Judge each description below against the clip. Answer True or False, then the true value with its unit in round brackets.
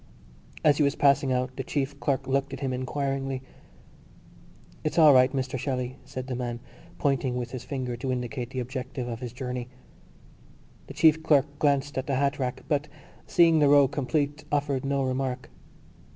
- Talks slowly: False (175 wpm)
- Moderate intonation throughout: False (2.0 semitones)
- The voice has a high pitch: False (135 Hz)